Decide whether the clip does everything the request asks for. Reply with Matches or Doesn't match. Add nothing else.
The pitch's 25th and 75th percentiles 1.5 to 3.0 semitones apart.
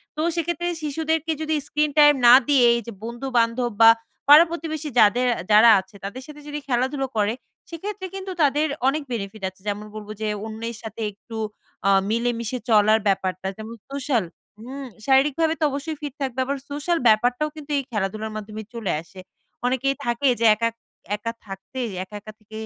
Doesn't match